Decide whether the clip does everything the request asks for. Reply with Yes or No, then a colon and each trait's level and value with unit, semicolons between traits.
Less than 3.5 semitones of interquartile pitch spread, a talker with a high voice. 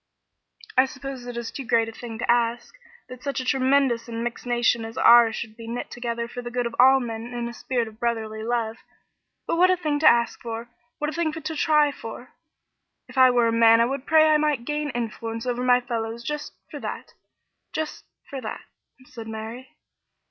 Yes: narrow, 2.6 semitones; high, 240 Hz